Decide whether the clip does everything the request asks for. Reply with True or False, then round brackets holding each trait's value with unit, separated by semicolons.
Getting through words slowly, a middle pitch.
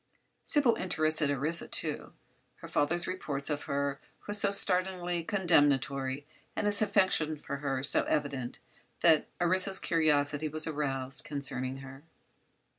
True (125 wpm; 150 Hz)